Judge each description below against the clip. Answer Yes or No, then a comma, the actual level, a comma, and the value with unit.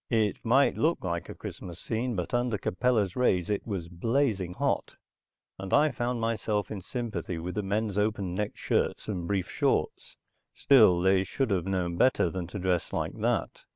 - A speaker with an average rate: Yes, average, 180 wpm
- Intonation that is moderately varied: Yes, average, 4.2 semitones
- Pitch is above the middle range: No, low, 100 Hz